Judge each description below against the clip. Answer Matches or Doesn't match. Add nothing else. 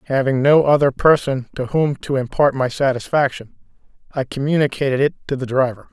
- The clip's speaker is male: Matches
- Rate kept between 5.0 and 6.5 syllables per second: Matches